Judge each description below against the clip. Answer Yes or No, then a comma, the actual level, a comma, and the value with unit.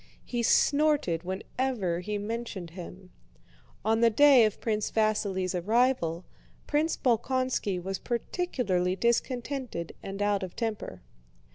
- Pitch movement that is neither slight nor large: Yes, average, 5.0 semitones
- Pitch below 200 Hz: No, high, 215 Hz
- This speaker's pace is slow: Yes, slow, 115 wpm